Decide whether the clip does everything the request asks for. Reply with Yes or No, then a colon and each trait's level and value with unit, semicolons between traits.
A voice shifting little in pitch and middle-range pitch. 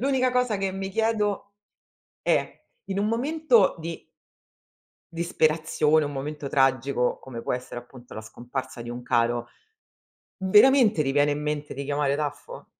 No: wide, 7.5 semitones; medium, 150 Hz